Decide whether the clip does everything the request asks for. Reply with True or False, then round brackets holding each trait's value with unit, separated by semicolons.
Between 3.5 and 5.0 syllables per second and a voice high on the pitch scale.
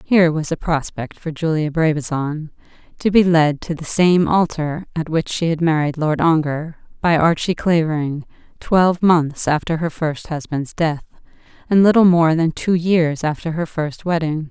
False (4.6 syllables/s; 160 Hz)